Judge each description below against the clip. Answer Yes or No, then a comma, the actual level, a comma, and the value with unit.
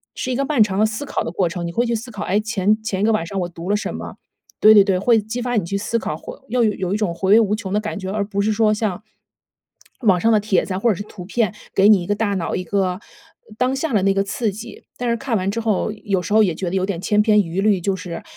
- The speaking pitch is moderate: No, high, 205 Hz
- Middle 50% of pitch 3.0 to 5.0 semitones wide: No, narrow, 2.6 semitones